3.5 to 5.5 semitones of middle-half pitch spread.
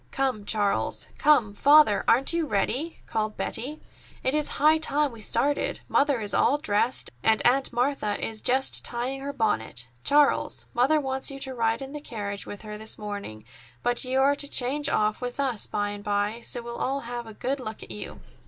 Yes: average, 4.7 semitones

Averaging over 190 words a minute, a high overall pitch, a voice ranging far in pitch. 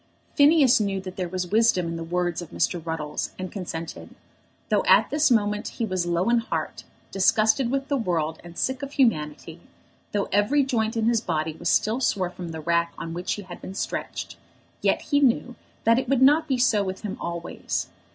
Yes: average, 200 wpm; high, 195 Hz; wide, 5.8 semitones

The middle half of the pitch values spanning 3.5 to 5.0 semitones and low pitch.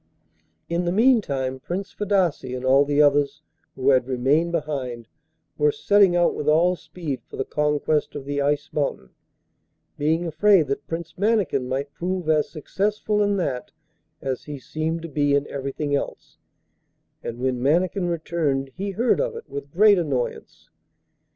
No: average, 4.6 semitones; medium, 150 Hz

